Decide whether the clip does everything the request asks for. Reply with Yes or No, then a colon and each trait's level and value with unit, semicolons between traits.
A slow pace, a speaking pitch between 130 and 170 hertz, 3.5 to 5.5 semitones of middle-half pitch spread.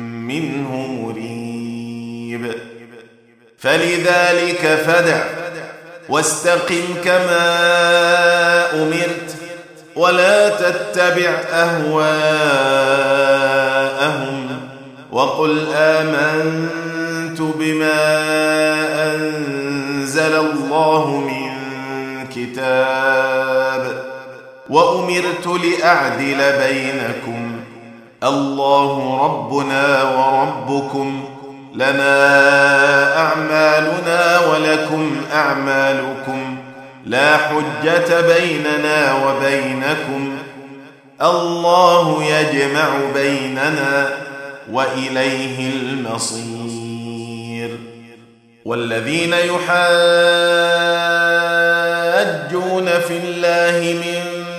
Yes: slow, 45 wpm; medium, 140 Hz; average, 4.2 semitones